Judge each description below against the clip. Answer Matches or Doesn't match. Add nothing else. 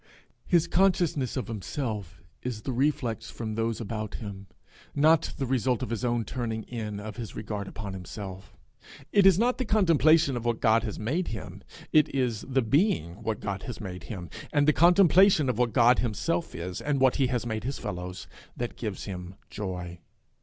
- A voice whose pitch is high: Doesn't match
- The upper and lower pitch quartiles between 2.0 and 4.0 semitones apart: Doesn't match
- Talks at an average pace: Matches